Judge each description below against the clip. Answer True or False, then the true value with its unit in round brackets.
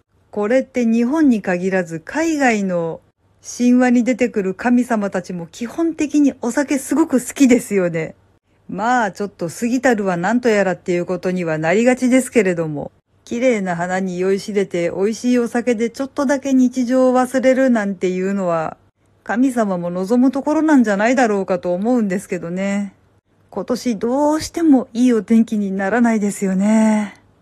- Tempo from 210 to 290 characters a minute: False (345 characters per minute)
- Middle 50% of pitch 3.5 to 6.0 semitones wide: True (5.2 semitones)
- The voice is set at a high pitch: True (225 Hz)